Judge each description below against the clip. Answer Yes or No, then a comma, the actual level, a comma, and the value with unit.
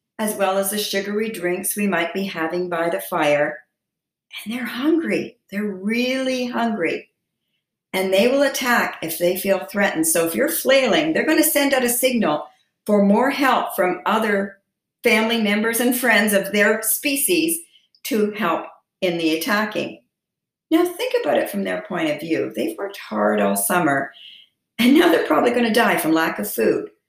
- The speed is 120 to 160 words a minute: No, average, 175 wpm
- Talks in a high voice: Yes, high, 210 Hz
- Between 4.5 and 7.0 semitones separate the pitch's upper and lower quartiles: Yes, wide, 5.4 semitones